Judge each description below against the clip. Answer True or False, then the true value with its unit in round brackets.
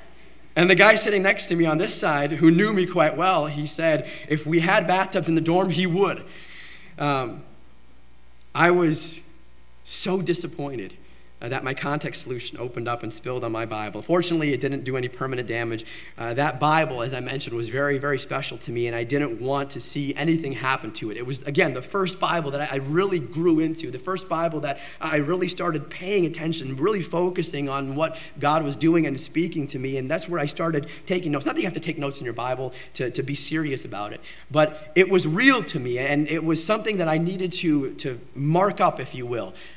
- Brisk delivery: True (220 wpm)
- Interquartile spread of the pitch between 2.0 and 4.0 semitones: False (4.4 semitones)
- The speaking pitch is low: False (150 Hz)